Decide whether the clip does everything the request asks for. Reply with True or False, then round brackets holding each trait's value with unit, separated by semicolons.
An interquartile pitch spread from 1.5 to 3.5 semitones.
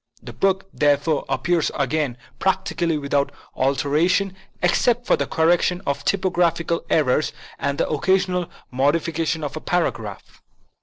False (3.9 semitones)